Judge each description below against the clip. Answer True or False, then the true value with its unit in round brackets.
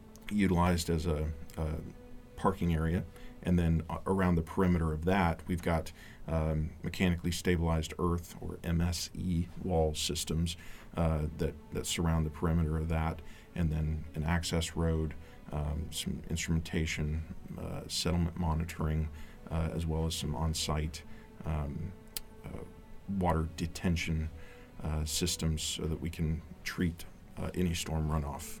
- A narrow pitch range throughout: True (1.7 semitones)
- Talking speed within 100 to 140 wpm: True (135 wpm)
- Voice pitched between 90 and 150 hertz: False (80 Hz)